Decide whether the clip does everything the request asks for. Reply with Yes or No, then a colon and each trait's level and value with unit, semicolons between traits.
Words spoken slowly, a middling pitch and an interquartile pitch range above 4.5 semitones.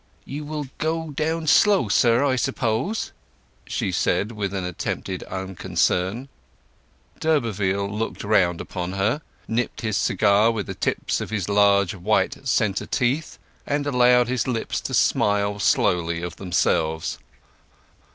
No: slow, 130 wpm; low, 110 Hz; average, 5.1 semitones